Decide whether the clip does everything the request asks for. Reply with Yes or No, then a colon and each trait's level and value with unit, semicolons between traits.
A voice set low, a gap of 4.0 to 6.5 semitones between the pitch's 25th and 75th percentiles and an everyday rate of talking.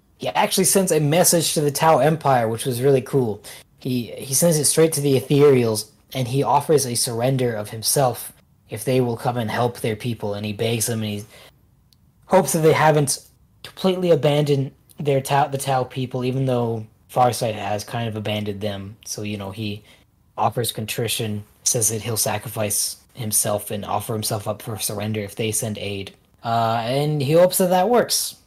Yes: low, 120 Hz; average, 4.8 semitones; average, 190 wpm